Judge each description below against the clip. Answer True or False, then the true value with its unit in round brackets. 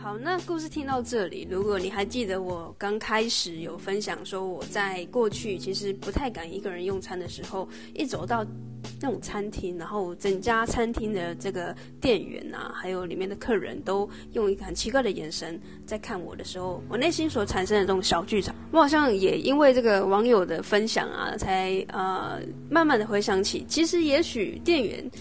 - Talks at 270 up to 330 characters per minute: True (290 characters per minute)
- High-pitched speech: True (200 Hz)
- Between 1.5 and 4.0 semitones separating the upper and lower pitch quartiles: True (3.7 semitones)